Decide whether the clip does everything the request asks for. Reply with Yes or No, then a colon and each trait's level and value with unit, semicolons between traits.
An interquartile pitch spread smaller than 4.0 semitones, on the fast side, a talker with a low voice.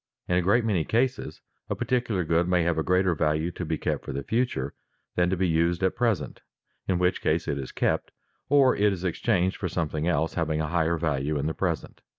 Yes: average, 3.1 semitones; fast, 220 wpm; very low, 85 Hz